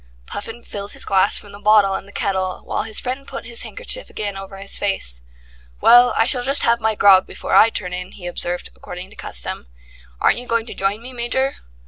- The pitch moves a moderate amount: Yes, average, 3.6 semitones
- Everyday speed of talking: No, fast, 215 wpm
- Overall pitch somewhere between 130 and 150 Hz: No, high, 205 Hz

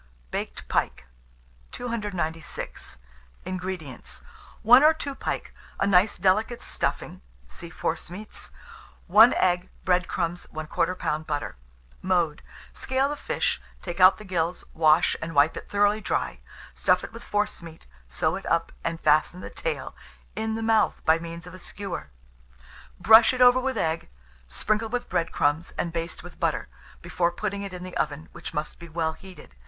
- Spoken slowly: No, average, 160 wpm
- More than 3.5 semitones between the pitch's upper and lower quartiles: Yes, average, 4.5 semitones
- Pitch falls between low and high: Yes, medium, 180 Hz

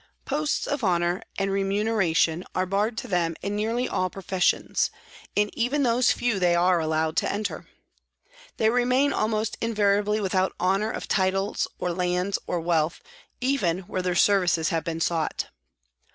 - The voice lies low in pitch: No, high, 195 Hz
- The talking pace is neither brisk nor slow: Yes, average, 150 wpm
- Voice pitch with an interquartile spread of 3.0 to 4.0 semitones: Yes, average, 3.6 semitones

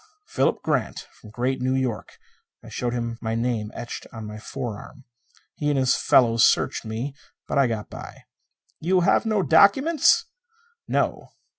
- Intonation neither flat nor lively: Yes, average, 4.2 semitones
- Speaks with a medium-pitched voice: No, low, 125 Hz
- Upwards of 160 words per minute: No, average, 155 wpm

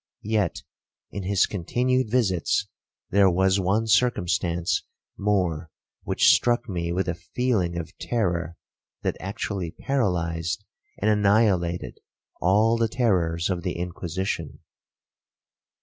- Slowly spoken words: Yes, slow, 110 wpm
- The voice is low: Yes, very low, 95 Hz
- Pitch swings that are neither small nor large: Yes, average, 3.9 semitones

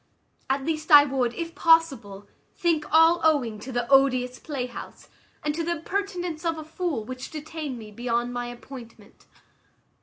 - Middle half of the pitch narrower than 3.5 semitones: No, average, 5.1 semitones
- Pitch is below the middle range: No, very high, 280 Hz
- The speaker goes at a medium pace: Yes, average, 155 wpm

